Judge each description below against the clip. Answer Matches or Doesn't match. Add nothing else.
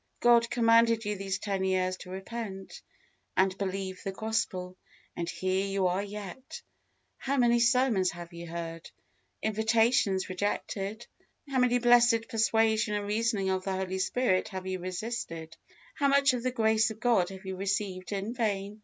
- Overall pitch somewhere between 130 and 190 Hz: Doesn't match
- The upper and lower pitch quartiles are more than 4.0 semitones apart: Doesn't match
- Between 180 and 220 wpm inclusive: Doesn't match